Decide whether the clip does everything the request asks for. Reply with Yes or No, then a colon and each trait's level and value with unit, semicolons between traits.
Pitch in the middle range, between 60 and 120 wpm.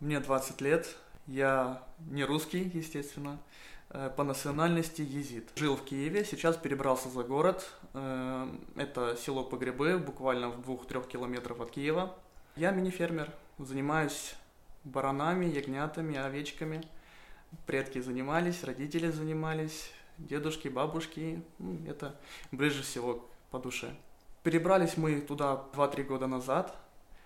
Yes: medium, 145 Hz; slow, 110 wpm